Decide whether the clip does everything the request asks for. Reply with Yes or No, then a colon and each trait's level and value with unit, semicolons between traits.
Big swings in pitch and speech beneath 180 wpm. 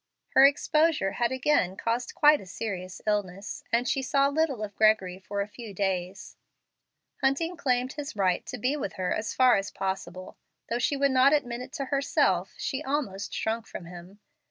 No: wide, 6.1 semitones; average, 190 wpm